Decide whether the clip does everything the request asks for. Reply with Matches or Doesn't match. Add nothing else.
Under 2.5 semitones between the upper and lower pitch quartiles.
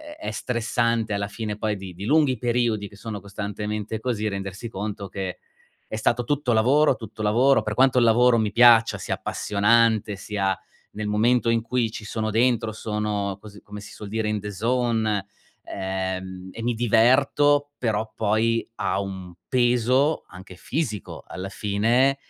Doesn't match